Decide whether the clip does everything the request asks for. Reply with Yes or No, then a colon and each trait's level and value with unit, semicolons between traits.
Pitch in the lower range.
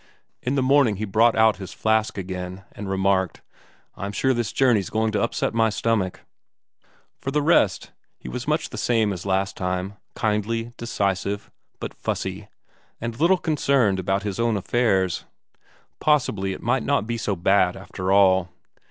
Yes: low, 105 Hz